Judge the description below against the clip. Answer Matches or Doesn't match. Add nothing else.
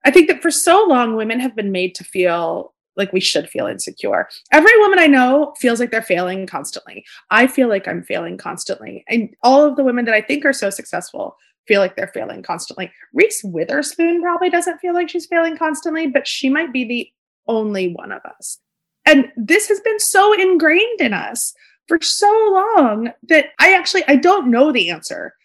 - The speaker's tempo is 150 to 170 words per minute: Doesn't match